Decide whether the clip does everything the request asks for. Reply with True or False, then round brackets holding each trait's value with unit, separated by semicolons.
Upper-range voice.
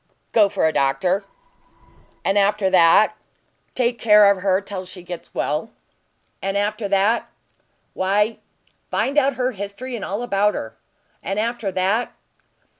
True (200 Hz)